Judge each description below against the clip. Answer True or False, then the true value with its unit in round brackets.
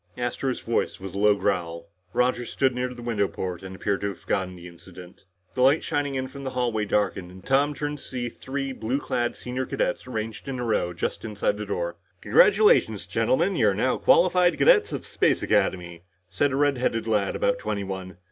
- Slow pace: False (200 wpm)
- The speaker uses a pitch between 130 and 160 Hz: False (115 Hz)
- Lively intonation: True (5.8 semitones)